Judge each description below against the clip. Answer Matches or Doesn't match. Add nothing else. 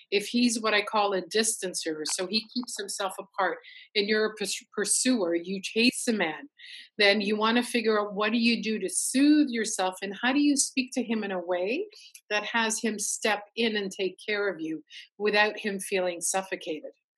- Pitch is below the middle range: Doesn't match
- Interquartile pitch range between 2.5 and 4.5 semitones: Matches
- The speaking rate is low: Doesn't match